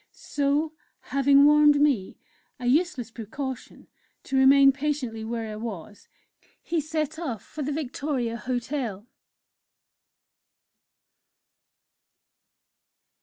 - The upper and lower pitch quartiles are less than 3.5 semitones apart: No, average, 4.1 semitones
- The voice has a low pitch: No, very high, 275 Hz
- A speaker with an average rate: No, slow, 90 wpm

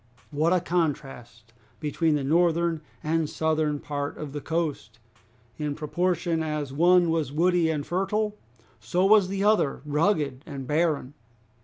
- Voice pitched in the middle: Yes, medium, 160 Hz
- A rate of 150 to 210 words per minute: No, average, 140 wpm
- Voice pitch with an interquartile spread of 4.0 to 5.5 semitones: No, average, 3.2 semitones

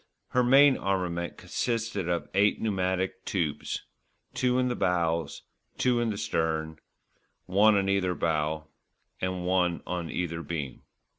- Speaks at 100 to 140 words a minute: Yes, slow, 135 wpm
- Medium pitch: No, very low, 90 Hz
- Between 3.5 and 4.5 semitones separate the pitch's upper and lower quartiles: Yes, average, 4.2 semitones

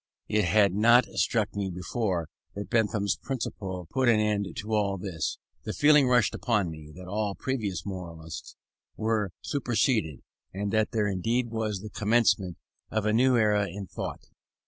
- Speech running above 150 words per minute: Yes, average, 160 wpm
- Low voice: Yes, low, 105 Hz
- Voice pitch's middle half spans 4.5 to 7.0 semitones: No, average, 3.1 semitones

